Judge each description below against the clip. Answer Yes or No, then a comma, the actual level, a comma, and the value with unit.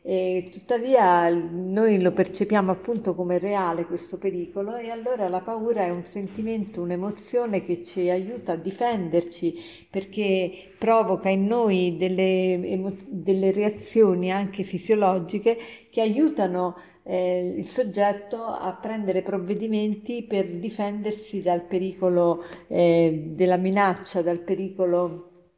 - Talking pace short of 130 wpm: Yes, slow, 115 wpm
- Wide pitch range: No, average, 2.7 semitones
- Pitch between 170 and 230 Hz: Yes, high, 190 Hz